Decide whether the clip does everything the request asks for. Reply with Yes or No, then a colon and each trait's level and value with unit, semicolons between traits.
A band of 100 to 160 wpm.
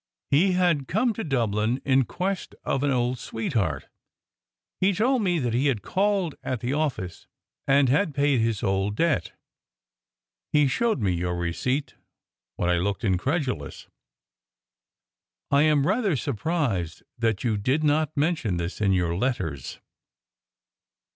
Yes: average, 140 wpm